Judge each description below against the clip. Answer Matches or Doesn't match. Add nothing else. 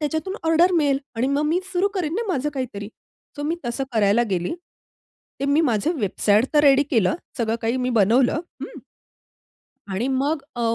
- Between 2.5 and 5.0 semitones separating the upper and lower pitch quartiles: Doesn't match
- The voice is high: Matches